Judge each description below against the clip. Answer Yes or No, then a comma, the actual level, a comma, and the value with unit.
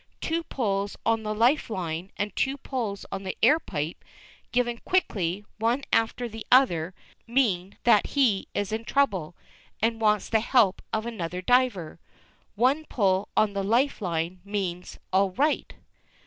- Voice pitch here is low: No, high, 215 Hz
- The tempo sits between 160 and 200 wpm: No, average, 150 wpm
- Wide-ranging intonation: No, average, 4.6 semitones